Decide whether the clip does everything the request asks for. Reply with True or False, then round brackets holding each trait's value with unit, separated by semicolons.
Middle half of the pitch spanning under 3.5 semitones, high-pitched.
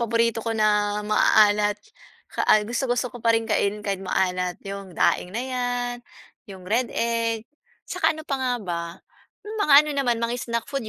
True (3.0 semitones; 230 Hz)